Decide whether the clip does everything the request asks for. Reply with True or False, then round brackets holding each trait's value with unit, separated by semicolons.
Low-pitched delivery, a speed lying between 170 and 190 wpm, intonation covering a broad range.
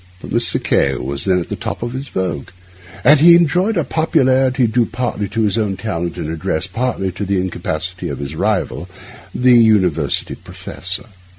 True (100 Hz; 175 wpm; 6.0 semitones)